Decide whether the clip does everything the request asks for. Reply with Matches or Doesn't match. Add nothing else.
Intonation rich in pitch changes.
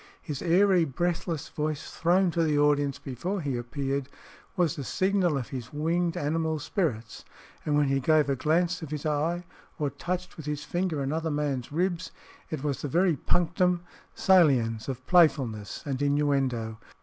Doesn't match